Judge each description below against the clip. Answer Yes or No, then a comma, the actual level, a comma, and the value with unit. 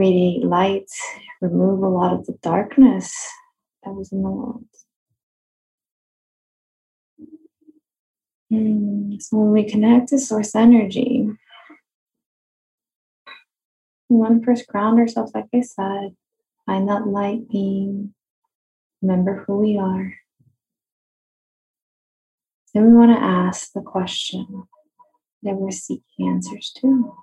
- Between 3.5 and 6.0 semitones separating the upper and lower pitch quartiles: Yes, average, 4.2 semitones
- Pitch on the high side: Yes, high, 215 Hz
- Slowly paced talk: Yes, slow, 110 wpm